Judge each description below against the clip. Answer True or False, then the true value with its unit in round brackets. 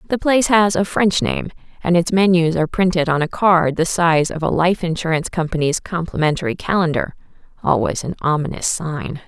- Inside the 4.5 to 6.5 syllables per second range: True (5.5 syllables/s)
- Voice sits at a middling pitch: True (170 Hz)